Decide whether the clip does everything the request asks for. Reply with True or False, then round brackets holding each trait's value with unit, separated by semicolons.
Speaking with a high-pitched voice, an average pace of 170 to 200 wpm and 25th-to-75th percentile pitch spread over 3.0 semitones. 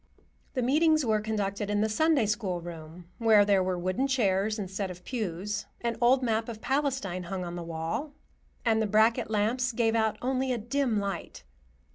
True (215 Hz; 180 wpm; 4.2 semitones)